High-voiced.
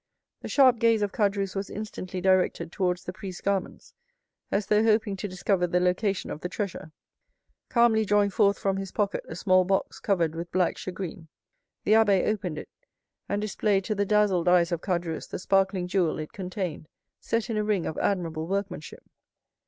Yes: high, 195 Hz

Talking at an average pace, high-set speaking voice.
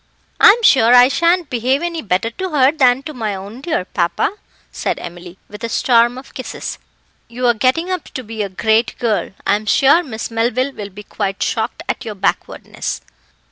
Yes: average, 180 wpm; high, 240 Hz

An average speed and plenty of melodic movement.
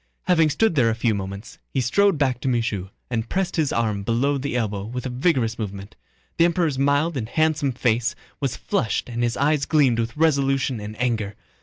No: average, 195 wpm; average, 4.3 semitones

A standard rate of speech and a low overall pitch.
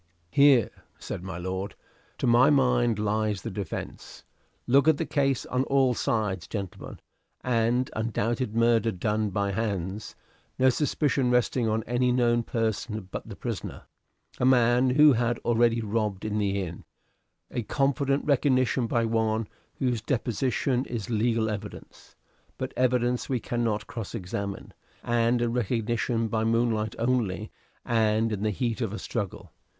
Yes: average, 145 wpm; low, 115 Hz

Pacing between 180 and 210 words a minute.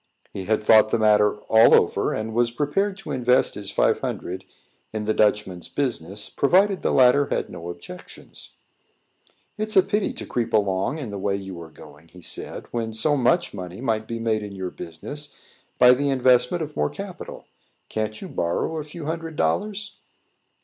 Yes: average, 185 wpm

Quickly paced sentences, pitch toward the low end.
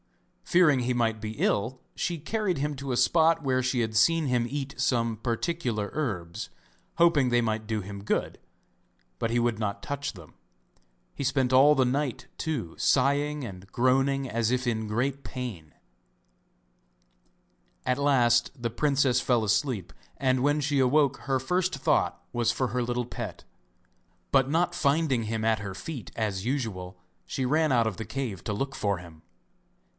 No: average, 165 wpm; low, 125 Hz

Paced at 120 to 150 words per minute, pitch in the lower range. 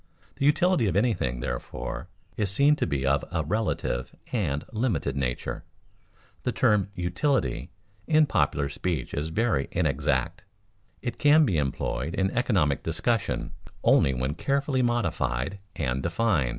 Yes: slow, 135 wpm; very low, 90 Hz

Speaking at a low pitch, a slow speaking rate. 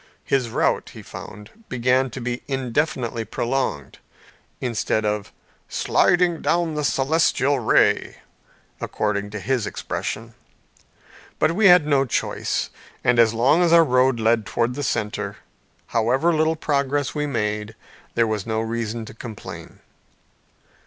Yes: low, 125 Hz; slow, 130 wpm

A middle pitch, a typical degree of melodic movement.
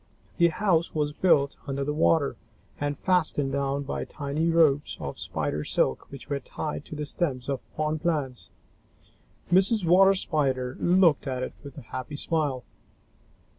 Yes: medium, 145 Hz; average, 3.3 semitones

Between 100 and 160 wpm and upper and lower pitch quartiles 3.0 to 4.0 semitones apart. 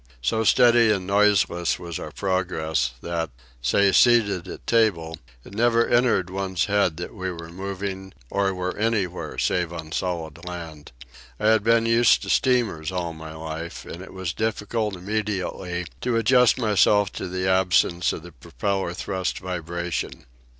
Yes: average, 155 wpm; average, 3.5 semitones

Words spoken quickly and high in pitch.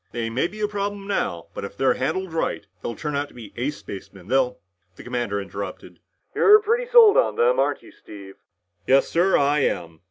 No: fast, 210 wpm; low, 135 Hz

